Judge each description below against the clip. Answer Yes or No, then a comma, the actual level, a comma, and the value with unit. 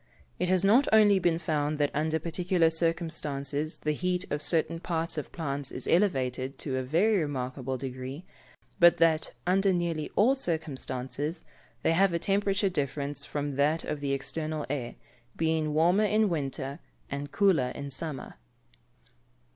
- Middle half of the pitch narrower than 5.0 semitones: Yes, average, 3.8 semitones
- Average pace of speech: Yes, average, 150 wpm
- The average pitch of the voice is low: No, medium, 155 Hz